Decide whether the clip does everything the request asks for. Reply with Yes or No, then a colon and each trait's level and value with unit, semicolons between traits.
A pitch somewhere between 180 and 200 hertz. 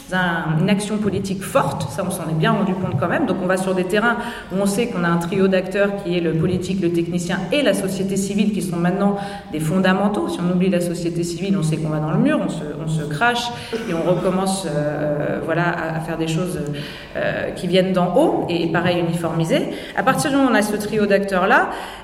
Yes: medium, 185 Hz